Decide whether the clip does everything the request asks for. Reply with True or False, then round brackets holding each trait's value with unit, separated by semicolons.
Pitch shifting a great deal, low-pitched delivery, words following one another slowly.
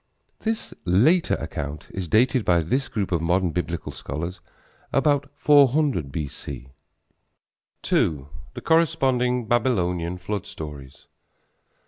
True (8.0 semitones; 95 Hz; 105 wpm)